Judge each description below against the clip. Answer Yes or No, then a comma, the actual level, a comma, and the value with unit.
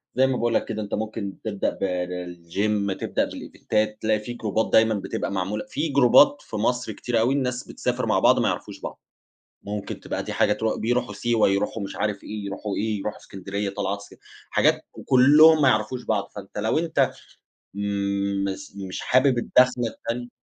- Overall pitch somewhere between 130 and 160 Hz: No, low, 110 Hz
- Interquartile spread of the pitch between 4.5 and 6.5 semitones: No, average, 3.5 semitones